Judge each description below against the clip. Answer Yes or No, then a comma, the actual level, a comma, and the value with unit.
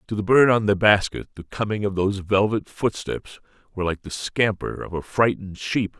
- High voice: No, low, 100 Hz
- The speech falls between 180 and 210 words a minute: Yes, average, 200 wpm